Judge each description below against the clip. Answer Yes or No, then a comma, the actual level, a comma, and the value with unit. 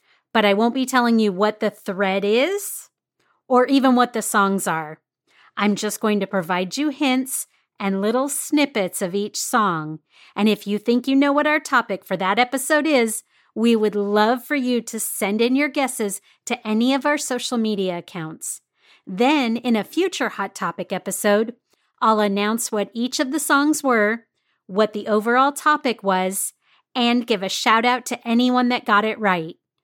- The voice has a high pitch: Yes, high, 225 Hz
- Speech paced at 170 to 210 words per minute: Yes, average, 180 wpm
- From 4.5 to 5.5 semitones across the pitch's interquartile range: No, average, 3.9 semitones